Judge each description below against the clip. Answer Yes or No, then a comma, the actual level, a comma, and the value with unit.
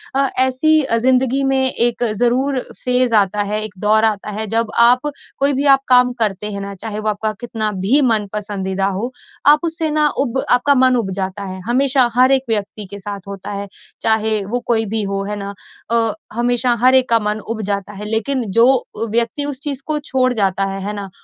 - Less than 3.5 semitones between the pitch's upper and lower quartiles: No, average, 3.8 semitones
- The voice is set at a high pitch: Yes, high, 225 Hz